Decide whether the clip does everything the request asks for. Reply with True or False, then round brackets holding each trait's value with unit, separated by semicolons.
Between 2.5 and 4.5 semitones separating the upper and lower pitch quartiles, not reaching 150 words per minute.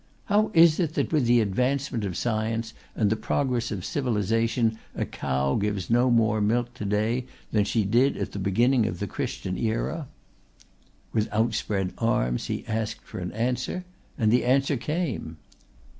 False (3.4 semitones; 165 wpm)